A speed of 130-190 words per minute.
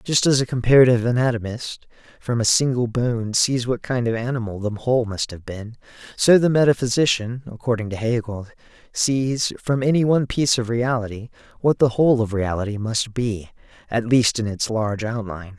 Yes: average, 170 wpm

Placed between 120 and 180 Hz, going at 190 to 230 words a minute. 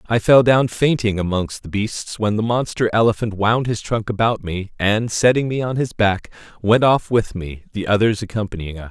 No: low, 110 Hz; average, 200 wpm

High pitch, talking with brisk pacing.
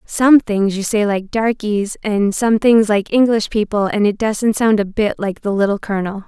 Yes: high, 210 Hz; fast, 210 wpm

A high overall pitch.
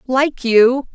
Yes: very high, 255 Hz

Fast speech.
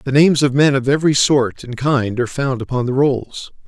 Yes: fast, 230 wpm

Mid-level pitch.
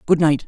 Yes: medium, 155 Hz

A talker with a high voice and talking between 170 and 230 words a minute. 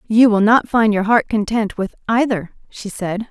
Yes: high, 215 Hz; average, 200 wpm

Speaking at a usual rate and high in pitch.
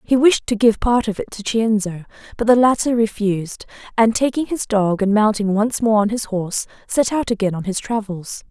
No: fast, 210 wpm; high, 220 Hz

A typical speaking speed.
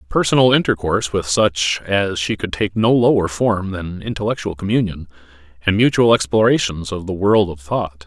Yes: average, 165 wpm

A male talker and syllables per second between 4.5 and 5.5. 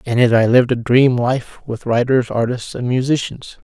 Yes: male; 4.9 syllables/s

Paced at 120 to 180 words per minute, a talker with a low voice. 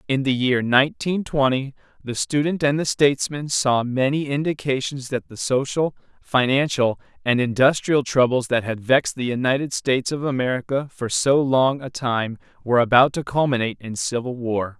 Yes: average, 160 wpm; low, 130 Hz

